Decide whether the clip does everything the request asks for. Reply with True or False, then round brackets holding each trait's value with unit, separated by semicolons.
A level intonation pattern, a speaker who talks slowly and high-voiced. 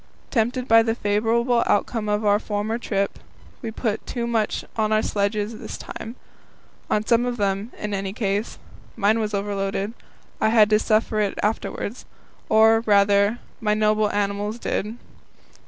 False (1.8 semitones; 155 wpm; 215 Hz)